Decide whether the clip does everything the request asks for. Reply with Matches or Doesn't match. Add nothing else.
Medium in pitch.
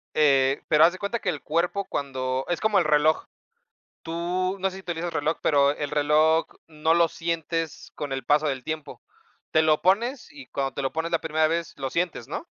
Matches